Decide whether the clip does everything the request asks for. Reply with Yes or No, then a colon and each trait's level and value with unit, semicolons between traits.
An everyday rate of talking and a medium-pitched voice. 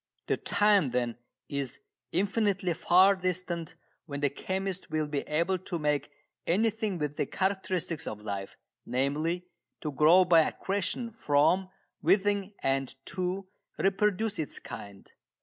No: slow, 130 wpm; medium, 175 Hz